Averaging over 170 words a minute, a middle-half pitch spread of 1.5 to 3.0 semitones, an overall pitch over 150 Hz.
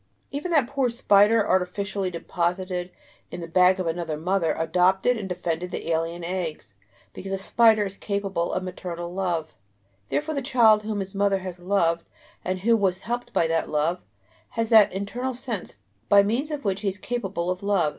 No: average, 180 wpm; average, 3.5 semitones; high, 190 Hz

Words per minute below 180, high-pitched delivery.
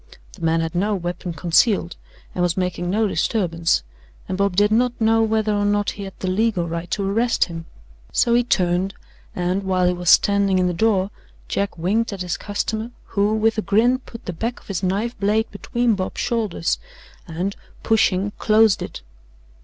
No: average, 185 wpm; high, 200 Hz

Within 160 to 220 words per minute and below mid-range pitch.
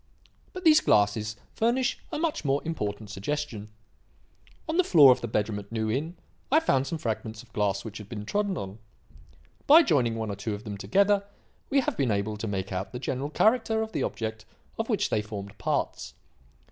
Yes: average, 195 wpm; low, 115 Hz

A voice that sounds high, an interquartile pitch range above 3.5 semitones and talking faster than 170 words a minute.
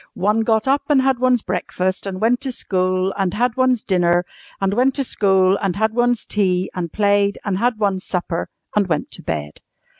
Yes: high, 200 Hz; average, 4.5 semitones; average, 200 wpm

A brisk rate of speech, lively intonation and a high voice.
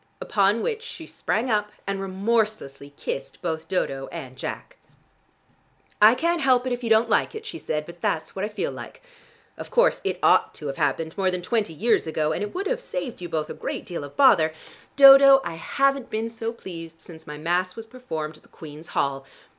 Yes: fast, 210 wpm; wide, 7.6 semitones; high, 200 Hz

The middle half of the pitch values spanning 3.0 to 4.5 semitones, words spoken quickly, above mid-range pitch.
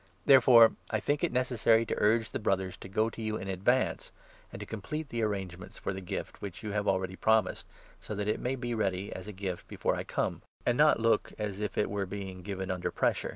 No: average, 3.3 semitones; fast, 235 wpm; low, 105 Hz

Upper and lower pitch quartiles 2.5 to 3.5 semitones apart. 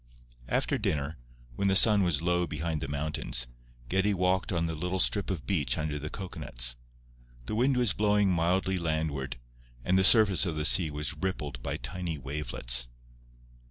No: average, 4.3 semitones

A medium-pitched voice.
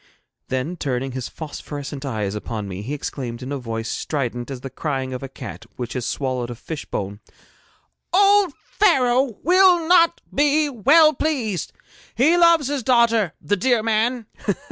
Yes: medium, 160 Hz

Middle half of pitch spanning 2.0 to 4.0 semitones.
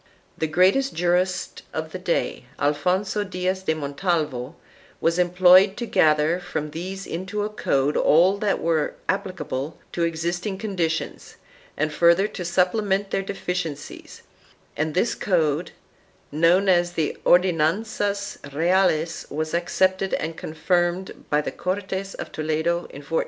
Yes: average, 3.1 semitones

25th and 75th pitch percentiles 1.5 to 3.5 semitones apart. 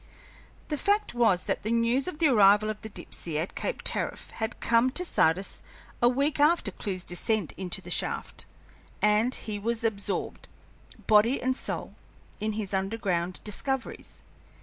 No: average, 4.2 semitones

